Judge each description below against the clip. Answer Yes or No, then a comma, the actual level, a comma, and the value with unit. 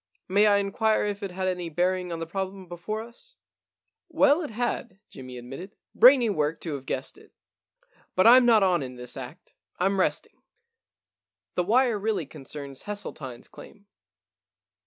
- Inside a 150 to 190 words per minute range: Yes, average, 180 wpm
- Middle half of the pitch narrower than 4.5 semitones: No, average, 5.0 semitones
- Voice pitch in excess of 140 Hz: Yes, high, 190 Hz